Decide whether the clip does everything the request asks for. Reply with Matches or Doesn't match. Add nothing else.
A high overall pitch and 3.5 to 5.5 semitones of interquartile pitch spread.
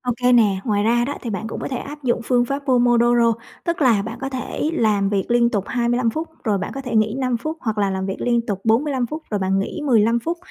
Doesn't match